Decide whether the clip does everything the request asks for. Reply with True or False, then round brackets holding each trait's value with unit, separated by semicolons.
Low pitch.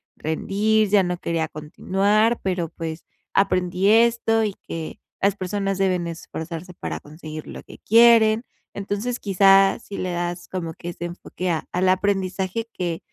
False (190 Hz)